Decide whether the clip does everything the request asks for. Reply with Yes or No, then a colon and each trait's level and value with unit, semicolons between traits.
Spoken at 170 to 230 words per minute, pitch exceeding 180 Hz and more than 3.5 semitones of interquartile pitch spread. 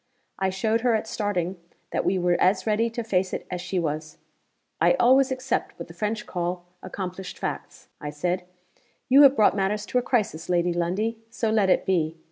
Yes: average, 195 wpm; high, 190 Hz; average, 4.1 semitones